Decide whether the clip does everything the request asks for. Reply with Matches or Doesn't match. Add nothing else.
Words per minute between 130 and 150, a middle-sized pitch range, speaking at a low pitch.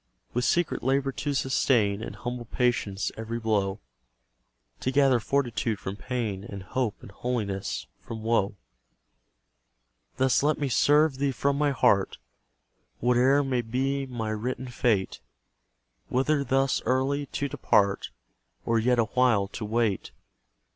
Matches